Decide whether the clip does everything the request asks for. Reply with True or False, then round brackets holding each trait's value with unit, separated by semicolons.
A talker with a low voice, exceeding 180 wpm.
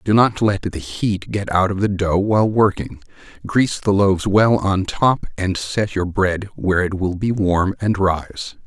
True (100 Hz; 200 wpm)